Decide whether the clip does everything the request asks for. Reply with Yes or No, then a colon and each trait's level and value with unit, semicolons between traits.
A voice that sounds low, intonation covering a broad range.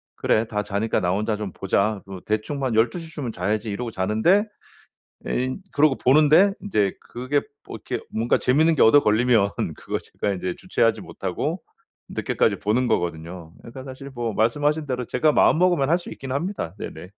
Yes: low, 120 Hz; wide, 5.7 semitones